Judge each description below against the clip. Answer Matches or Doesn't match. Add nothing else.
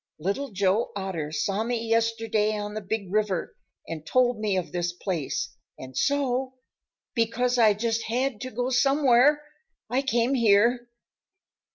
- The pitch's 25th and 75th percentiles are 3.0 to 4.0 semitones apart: Matches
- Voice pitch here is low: Doesn't match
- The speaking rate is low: Doesn't match